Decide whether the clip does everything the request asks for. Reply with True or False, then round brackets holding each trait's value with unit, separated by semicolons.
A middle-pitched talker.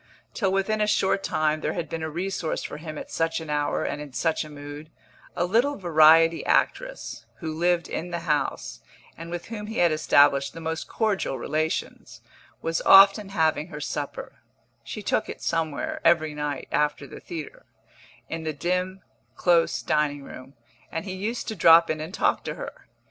True (165 Hz)